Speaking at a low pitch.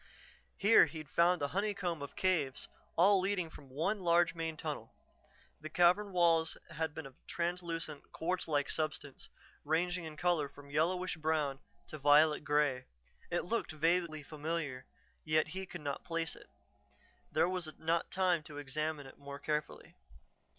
No: medium, 160 Hz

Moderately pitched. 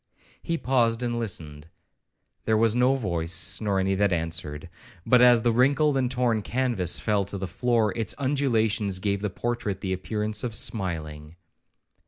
No: low, 105 Hz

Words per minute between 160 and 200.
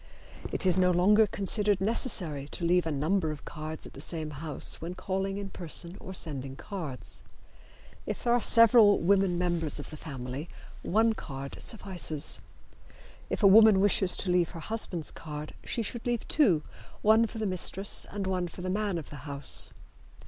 Yes: average, 180 wpm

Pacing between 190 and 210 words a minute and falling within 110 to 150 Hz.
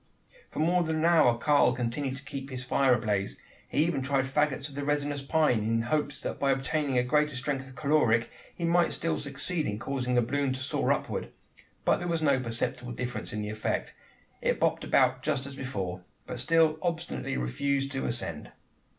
Yes: average, 195 wpm; low, 135 Hz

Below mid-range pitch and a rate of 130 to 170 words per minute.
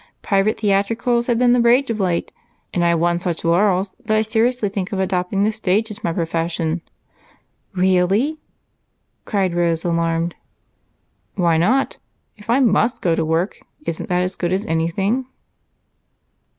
No: high, 190 Hz; average, 155 wpm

